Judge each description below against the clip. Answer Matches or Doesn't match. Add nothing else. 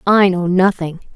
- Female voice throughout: Matches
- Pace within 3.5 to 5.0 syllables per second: Matches